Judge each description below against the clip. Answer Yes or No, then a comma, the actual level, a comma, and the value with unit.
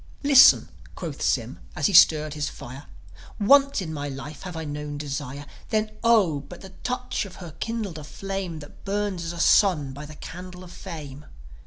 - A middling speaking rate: Yes, average, 185 wpm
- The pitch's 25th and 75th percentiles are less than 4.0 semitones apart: No, average, 5.3 semitones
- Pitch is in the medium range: Yes, medium, 170 Hz